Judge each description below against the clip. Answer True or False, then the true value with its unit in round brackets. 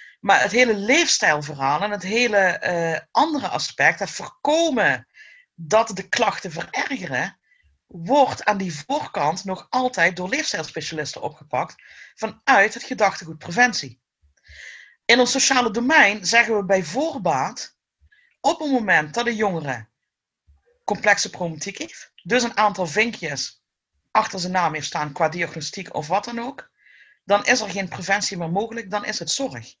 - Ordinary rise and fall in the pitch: False (6.2 semitones)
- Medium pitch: False (200 Hz)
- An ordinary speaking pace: True (145 wpm)